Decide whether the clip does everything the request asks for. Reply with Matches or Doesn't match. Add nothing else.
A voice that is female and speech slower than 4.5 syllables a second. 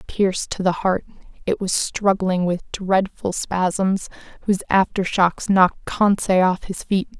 Matches